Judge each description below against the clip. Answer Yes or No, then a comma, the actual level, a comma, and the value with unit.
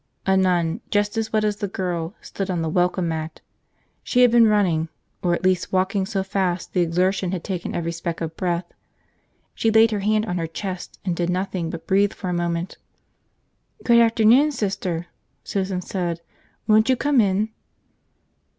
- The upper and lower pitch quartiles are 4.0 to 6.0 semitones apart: No, average, 3.4 semitones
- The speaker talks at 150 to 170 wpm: No, average, 180 wpm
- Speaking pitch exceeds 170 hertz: Yes, high, 190 Hz